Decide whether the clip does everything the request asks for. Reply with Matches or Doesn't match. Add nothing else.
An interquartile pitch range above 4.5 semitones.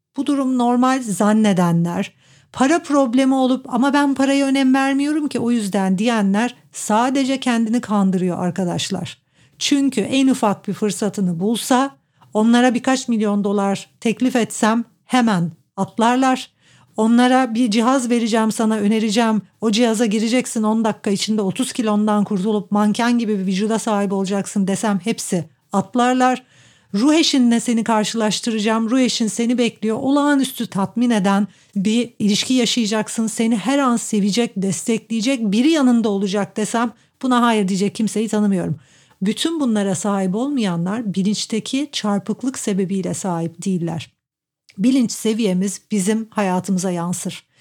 Doesn't match